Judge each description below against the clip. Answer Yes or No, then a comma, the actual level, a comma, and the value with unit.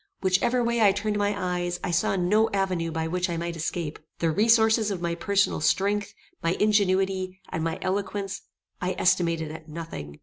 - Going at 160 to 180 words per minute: Yes, average, 175 wpm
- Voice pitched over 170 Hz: Yes, medium, 185 Hz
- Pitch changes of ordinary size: Yes, average, 3.3 semitones